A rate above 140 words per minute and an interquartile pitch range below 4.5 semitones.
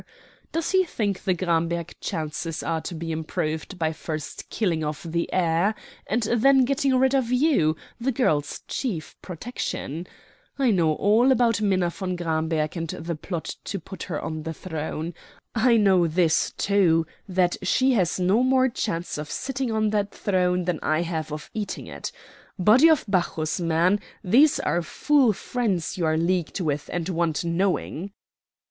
No: average, 165 wpm; wide, 5.4 semitones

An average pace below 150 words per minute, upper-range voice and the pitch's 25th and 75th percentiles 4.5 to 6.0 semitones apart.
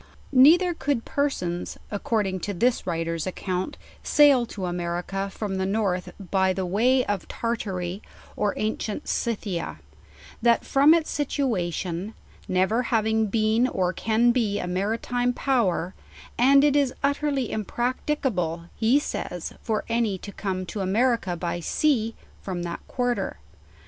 Yes: average, 140 wpm; high, 215 Hz; average, 5.1 semitones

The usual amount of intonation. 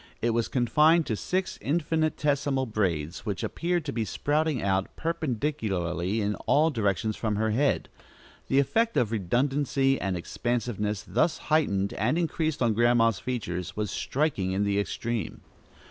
No: wide, 6.5 semitones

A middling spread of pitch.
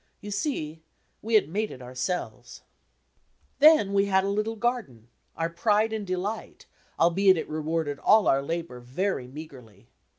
No: wide, 6.3 semitones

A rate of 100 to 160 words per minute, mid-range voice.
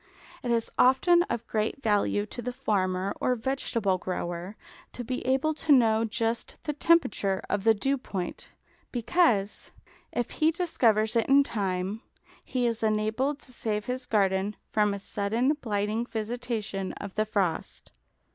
No: average, 150 wpm; high, 220 Hz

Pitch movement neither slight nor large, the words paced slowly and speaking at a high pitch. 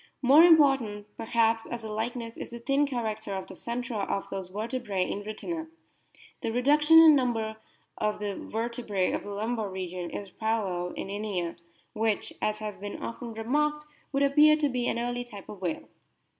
No: average, 3.5 semitones; average, 180 wpm; high, 225 Hz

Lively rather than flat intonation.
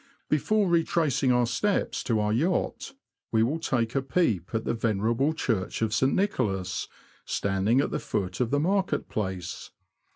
Yes: wide, 6.7 semitones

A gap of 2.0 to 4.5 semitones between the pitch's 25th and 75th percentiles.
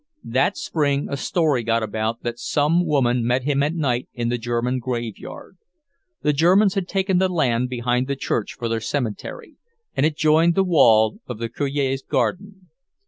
No: average, 5.0 semitones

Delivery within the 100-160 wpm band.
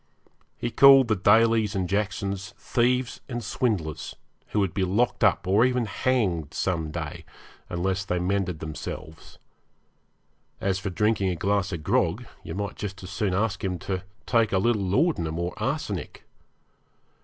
Yes: average, 155 wpm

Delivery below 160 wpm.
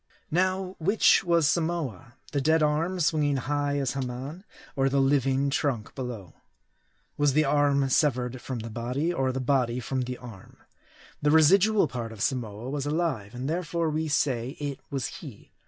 No: average, 165 wpm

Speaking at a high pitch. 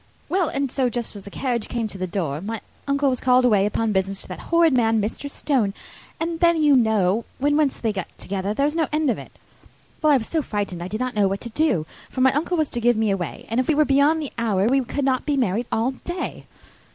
Yes: high, 245 Hz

